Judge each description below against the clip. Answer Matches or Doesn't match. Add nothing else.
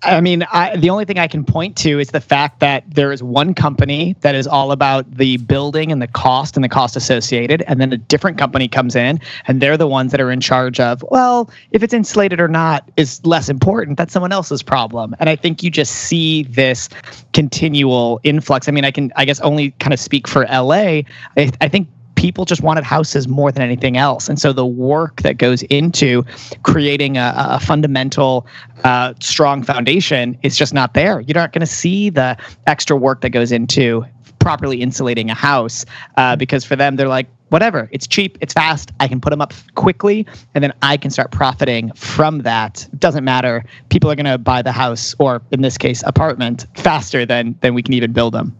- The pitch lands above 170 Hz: Doesn't match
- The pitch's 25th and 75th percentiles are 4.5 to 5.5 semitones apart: Doesn't match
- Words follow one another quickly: Matches